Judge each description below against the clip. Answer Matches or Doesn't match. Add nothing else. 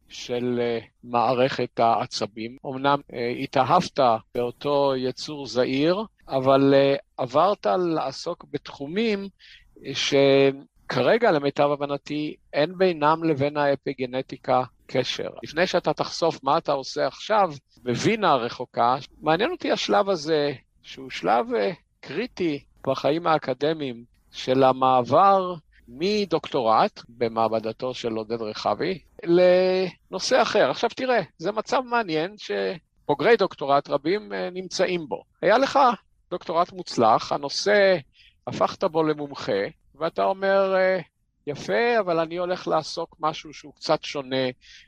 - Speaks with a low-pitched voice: Doesn't match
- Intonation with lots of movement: Matches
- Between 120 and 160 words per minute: Doesn't match